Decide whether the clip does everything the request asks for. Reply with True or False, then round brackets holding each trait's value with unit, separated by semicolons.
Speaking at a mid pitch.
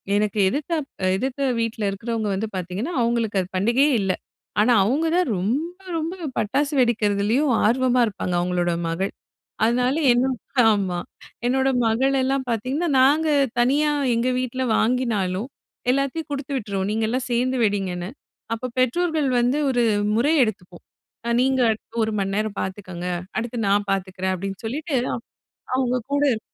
False (235 Hz)